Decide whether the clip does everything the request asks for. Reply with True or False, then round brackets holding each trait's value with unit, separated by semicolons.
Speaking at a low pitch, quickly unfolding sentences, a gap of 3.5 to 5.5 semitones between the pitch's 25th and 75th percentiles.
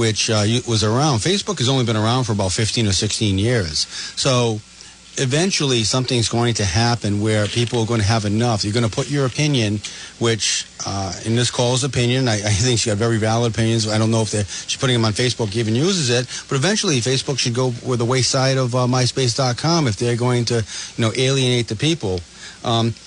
False (120 Hz; 210 wpm; 2.7 semitones)